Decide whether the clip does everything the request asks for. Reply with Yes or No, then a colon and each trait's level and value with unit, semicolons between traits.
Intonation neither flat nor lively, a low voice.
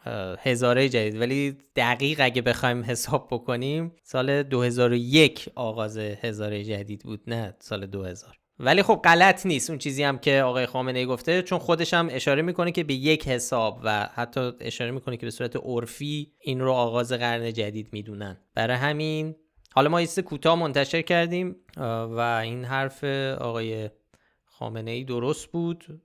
Yes: average, 4.5 semitones; low, 125 Hz